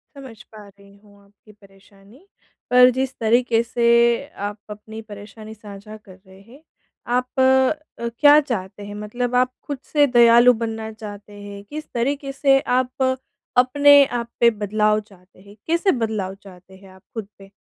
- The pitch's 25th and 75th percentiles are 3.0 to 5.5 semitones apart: Yes, average, 3.7 semitones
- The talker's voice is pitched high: Yes, high, 220 Hz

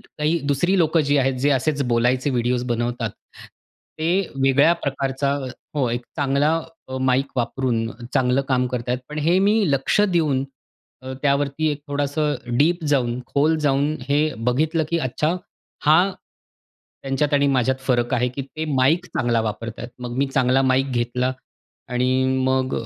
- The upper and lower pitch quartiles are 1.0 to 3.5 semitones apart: Yes, average, 3.0 semitones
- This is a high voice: No, low, 135 Hz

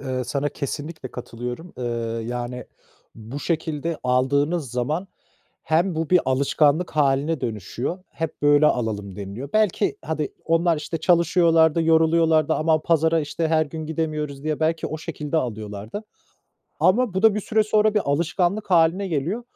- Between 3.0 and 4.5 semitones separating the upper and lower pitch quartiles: Yes, average, 3.6 semitones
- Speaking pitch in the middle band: Yes, medium, 155 Hz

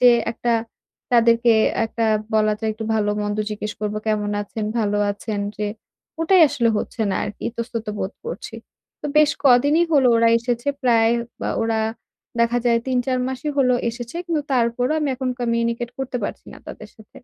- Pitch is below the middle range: No, high, 235 Hz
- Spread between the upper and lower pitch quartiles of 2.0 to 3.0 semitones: Yes, narrow, 2.5 semitones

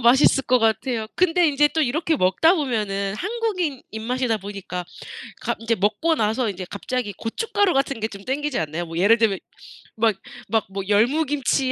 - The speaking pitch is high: Yes, high, 235 Hz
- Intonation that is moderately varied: No, wide, 6.2 semitones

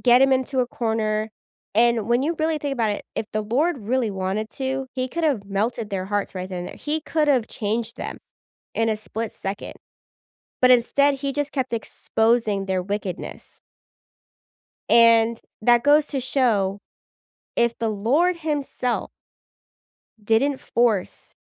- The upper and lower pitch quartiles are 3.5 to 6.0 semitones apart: Yes, average, 4.1 semitones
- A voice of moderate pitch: No, high, 235 Hz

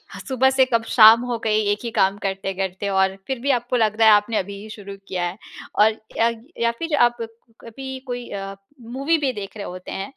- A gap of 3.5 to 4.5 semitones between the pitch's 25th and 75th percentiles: Yes, average, 3.8 semitones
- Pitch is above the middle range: Yes, high, 220 Hz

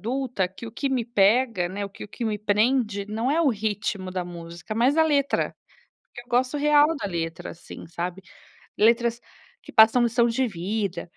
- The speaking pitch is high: Yes, high, 220 Hz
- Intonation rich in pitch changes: No, average, 4.5 semitones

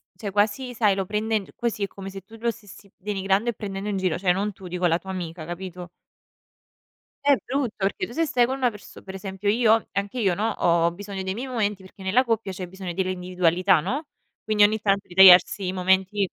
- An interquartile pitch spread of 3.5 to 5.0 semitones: No, narrow, 2.5 semitones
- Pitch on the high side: Yes, high, 195 Hz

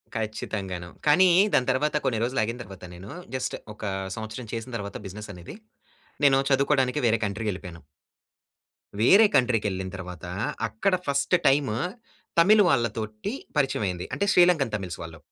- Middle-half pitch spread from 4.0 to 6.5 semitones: Yes, wide, 5.6 semitones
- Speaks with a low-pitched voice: Yes, low, 115 Hz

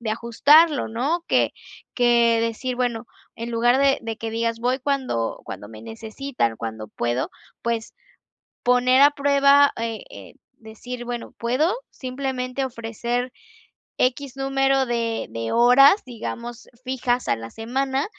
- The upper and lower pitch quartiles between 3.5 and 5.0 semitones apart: No, average, 2.8 semitones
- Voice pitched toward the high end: Yes, high, 245 Hz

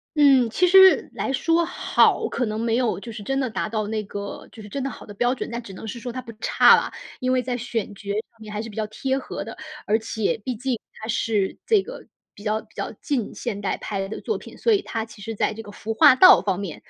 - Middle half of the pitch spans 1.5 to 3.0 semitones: No, average, 3.6 semitones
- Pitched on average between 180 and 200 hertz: No, high, 225 Hz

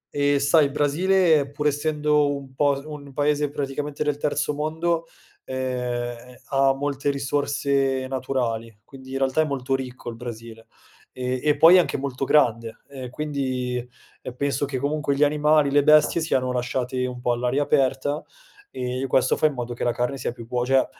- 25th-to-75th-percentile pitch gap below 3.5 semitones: Yes, narrow, 2.6 semitones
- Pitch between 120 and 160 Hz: Yes, low, 135 Hz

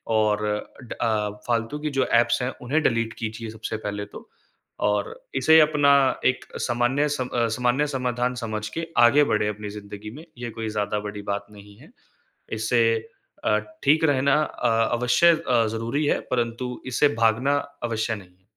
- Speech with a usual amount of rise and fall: Yes, average, 3.4 semitones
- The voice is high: No, low, 115 Hz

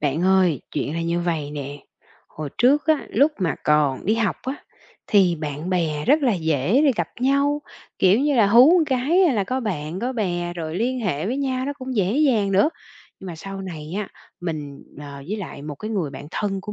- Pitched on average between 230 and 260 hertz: No, high, 190 Hz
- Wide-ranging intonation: Yes, wide, 8.2 semitones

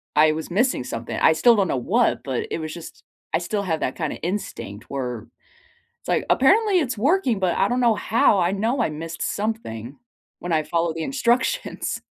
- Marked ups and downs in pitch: Yes, wide, 7.2 semitones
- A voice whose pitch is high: No, medium, 175 Hz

